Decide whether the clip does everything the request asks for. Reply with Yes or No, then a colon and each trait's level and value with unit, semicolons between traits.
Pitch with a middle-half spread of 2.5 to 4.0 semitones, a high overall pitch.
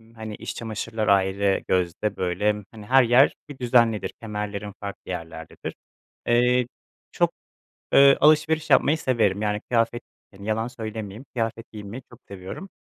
No: average, 3.3 semitones; low, 110 Hz